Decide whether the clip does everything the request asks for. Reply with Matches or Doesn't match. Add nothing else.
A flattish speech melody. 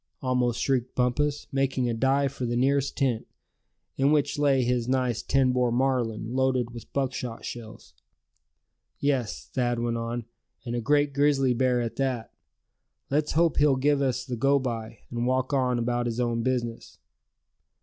Matches